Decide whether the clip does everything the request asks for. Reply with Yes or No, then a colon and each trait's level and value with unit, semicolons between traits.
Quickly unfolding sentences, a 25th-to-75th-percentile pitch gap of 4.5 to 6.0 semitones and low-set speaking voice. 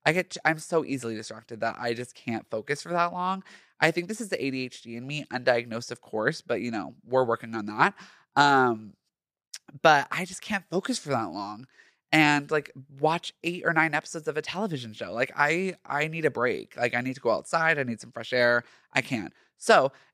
No: fast, 215 wpm; wide, 5.4 semitones; medium, 145 Hz